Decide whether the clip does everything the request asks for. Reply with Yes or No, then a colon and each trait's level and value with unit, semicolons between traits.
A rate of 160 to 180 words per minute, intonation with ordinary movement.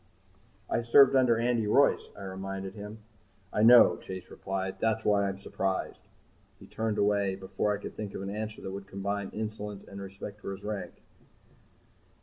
No: average, 170 wpm; narrow, 1.9 semitones